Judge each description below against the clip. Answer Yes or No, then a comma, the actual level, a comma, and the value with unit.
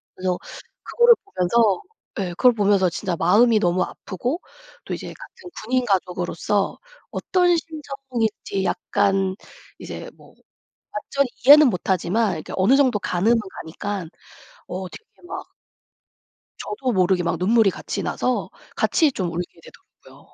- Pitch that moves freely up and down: Yes, wide, 5.8 semitones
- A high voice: Yes, high, 205 Hz